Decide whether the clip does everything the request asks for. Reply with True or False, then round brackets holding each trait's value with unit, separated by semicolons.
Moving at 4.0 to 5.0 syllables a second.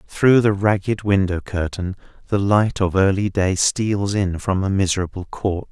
True (4.5 syllables/s)